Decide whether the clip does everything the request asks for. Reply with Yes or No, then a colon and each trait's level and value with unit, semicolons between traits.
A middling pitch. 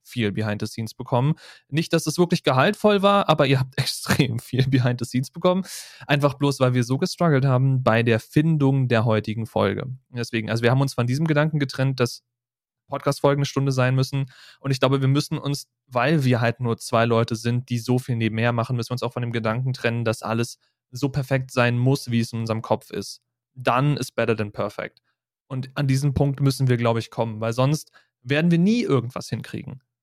No: low, 130 Hz